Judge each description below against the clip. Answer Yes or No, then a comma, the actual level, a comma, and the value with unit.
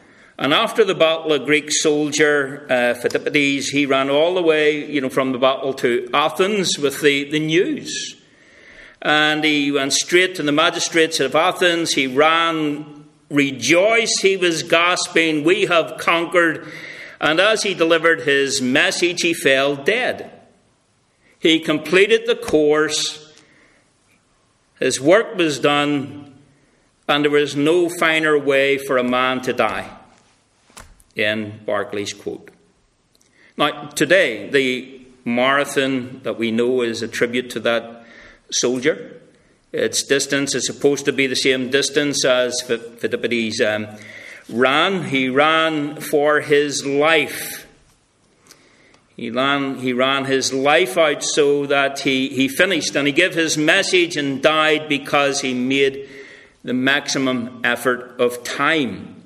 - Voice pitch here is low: No, medium, 145 Hz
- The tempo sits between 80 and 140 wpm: Yes, slow, 135 wpm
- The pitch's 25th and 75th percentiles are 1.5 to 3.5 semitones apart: Yes, average, 3.0 semitones